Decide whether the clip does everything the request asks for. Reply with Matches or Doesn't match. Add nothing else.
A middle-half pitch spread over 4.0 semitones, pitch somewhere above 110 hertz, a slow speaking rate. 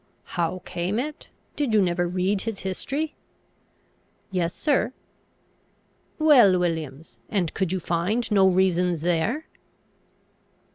Matches